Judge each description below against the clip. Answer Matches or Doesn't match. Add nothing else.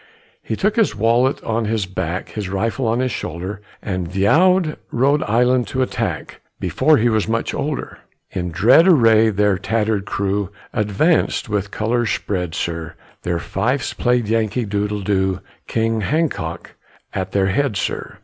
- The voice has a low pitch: Matches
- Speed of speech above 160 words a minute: Doesn't match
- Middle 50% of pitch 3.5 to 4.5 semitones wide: Matches